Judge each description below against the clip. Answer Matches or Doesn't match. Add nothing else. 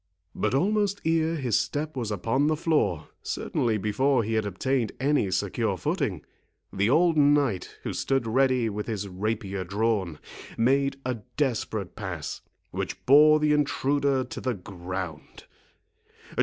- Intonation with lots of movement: Matches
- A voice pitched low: Matches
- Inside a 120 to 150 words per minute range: Matches